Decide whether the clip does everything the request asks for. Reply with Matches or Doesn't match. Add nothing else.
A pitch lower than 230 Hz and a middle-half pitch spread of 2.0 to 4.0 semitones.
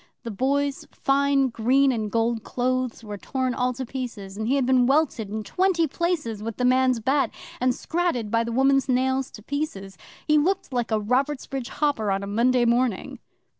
Doesn't match